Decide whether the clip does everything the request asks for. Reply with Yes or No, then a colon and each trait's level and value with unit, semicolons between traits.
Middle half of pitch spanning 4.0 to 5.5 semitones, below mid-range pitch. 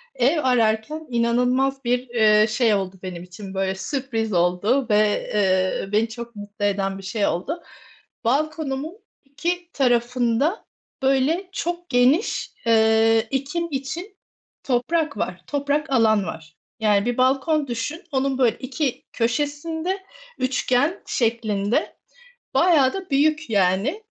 No: average, 5.2 semitones; very high, 250 Hz